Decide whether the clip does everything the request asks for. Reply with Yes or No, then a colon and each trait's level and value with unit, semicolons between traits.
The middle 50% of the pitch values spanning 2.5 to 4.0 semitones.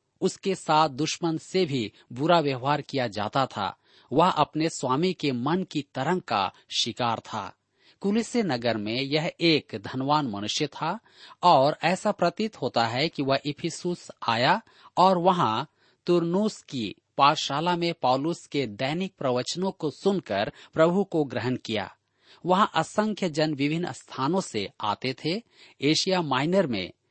No: average, 5.3 semitones